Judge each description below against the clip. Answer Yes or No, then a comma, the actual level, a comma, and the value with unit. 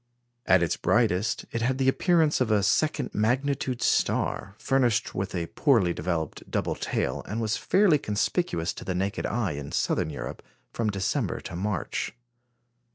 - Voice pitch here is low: Yes, low, 105 Hz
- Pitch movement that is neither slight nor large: No, wide, 6.2 semitones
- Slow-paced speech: No, average, 160 wpm